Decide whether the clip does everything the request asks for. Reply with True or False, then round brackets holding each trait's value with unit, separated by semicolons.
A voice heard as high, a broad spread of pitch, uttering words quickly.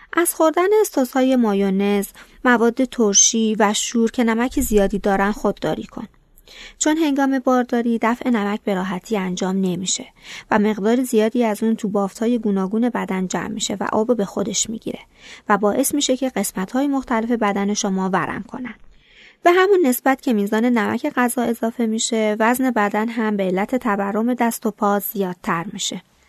False (220 Hz; 3.5 semitones; 160 wpm)